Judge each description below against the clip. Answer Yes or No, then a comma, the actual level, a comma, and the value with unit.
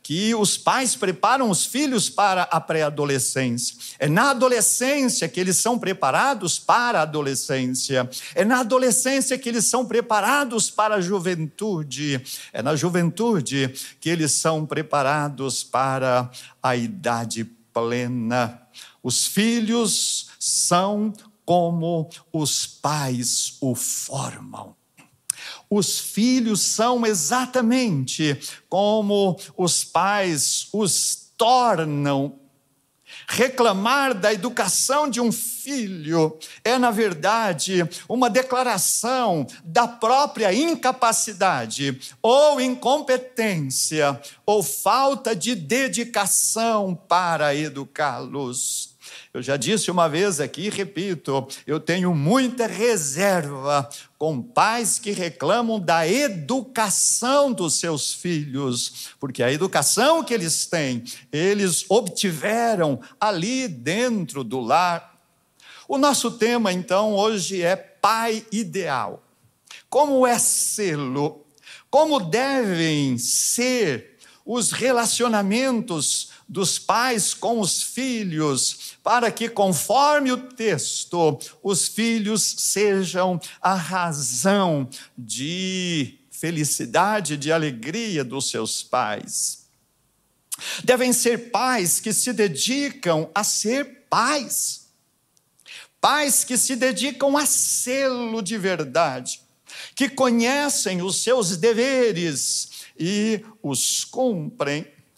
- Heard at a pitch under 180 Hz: No, high, 190 Hz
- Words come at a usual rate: No, slow, 100 wpm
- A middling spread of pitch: No, wide, 8.1 semitones